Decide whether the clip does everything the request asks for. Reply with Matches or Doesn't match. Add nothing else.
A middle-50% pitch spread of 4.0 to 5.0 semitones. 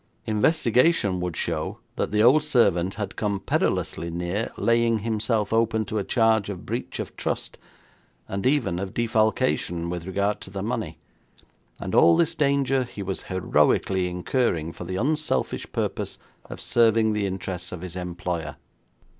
Matches